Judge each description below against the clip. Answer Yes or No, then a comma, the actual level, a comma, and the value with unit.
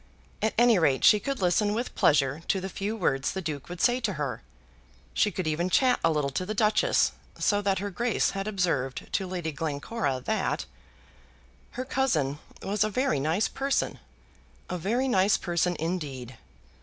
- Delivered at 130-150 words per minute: No, average, 175 wpm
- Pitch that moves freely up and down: Yes, wide, 5.9 semitones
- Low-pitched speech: No, medium, 185 Hz